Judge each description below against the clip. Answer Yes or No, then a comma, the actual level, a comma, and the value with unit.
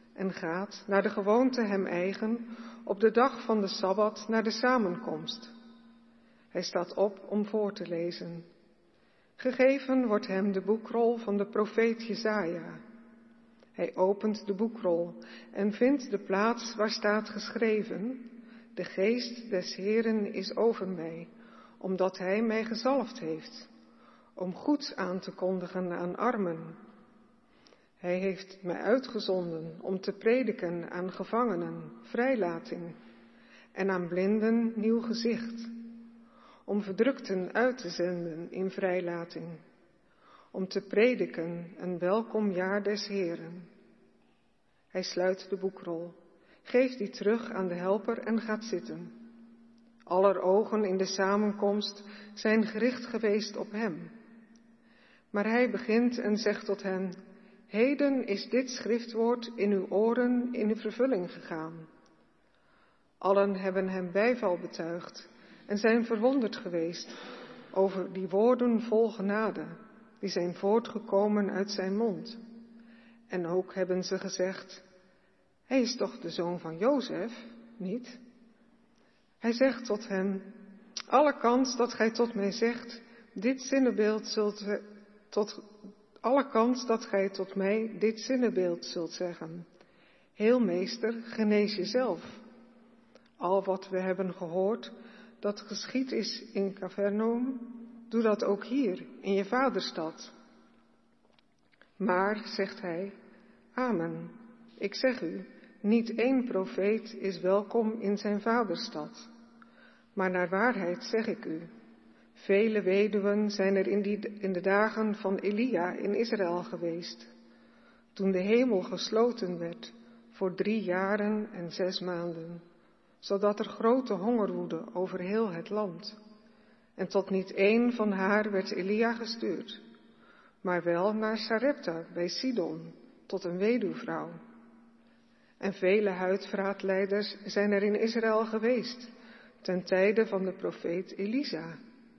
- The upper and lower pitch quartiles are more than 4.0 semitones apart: No, average, 3.5 semitones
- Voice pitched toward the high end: Yes, high, 210 Hz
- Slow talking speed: Yes, slow, 125 wpm